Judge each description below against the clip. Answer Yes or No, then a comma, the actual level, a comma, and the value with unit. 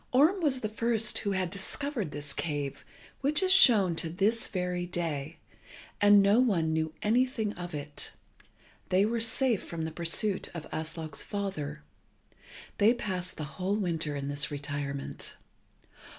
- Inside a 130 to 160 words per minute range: Yes, average, 150 wpm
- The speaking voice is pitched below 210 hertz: Yes, medium, 185 Hz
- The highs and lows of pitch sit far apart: Yes, wide, 5.9 semitones